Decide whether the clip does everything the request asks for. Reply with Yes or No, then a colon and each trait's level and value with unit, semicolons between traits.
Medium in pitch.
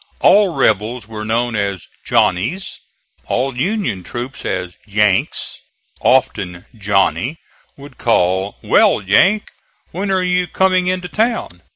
No: low, 120 Hz